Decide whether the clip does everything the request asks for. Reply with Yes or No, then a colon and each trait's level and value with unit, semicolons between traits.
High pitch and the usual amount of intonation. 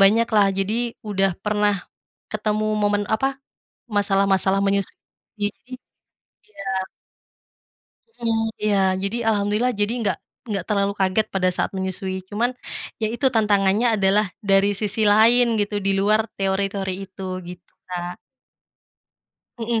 No: high, 205 Hz; narrow, 1.8 semitones